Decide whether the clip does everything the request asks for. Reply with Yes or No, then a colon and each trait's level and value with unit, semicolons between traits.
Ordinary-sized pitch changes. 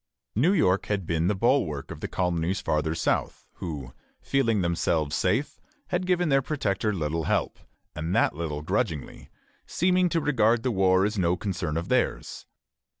No: wide, 7.9 semitones